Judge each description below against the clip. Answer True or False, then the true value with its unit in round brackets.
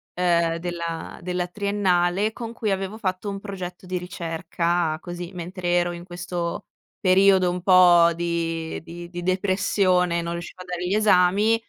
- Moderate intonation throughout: False (1.7 semitones)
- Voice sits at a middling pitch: True (180 Hz)